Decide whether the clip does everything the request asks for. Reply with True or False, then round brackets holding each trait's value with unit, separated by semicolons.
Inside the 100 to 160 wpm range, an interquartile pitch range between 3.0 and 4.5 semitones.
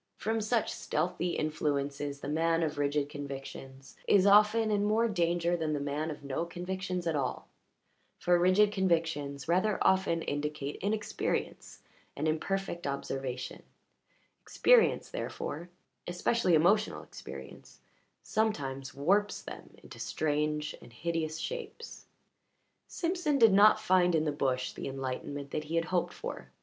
False (135 wpm; 5.5 semitones)